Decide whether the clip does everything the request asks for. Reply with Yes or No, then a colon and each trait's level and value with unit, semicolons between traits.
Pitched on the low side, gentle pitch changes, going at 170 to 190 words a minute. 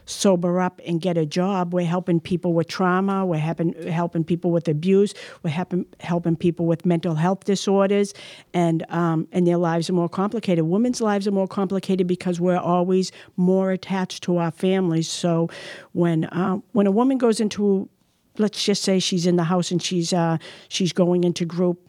No: medium, 180 Hz; narrow, 1.9 semitones; average, 185 wpm